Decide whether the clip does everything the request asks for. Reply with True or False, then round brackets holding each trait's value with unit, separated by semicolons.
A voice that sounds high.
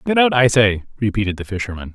False (115 Hz)